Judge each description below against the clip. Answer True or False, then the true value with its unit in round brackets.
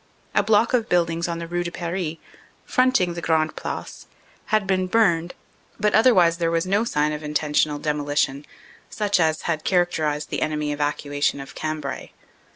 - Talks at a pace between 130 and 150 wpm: False (170 wpm)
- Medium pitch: True (165 Hz)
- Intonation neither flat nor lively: True (3.6 semitones)